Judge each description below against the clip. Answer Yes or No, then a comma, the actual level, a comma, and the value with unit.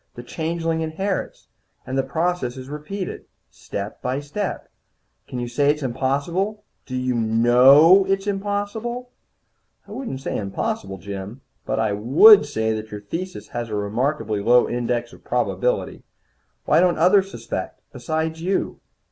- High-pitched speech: No, medium, 140 Hz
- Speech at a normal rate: Yes, average, 145 wpm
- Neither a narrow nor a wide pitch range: No, wide, 7.6 semitones